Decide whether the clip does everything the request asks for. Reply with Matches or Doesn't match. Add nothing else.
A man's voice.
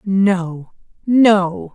Doesn't match